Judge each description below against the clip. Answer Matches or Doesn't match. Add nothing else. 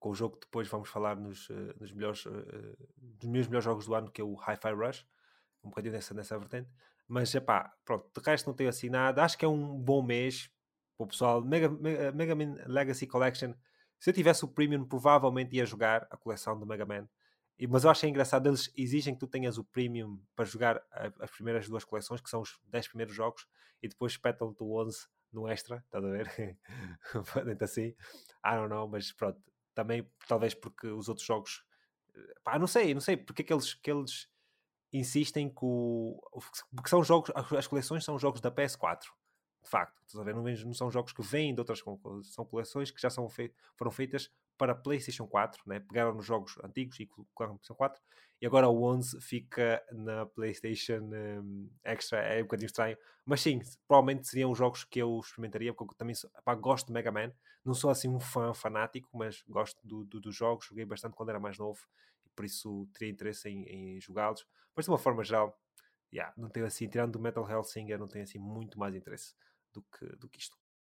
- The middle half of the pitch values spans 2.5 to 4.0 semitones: Matches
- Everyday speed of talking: Doesn't match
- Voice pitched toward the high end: Doesn't match